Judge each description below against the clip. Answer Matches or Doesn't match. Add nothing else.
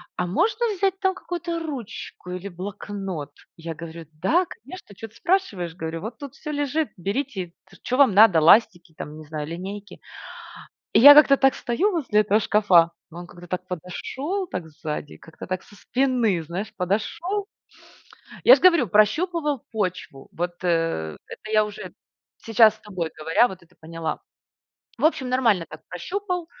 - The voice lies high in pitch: Matches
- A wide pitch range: Matches